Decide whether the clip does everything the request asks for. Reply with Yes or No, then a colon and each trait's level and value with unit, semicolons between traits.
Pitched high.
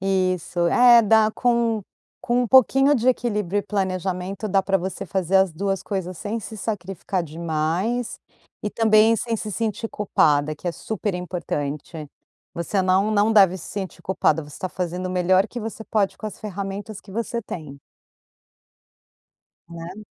Yes: high, 195 Hz